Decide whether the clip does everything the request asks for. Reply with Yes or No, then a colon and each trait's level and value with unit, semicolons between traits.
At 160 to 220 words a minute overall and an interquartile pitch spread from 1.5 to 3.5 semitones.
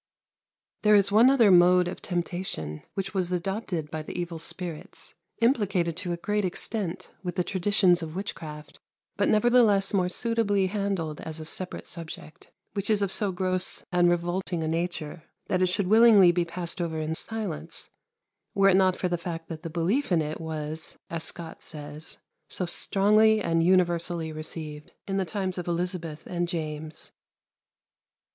Yes: average, 165 wpm; average, 3.1 semitones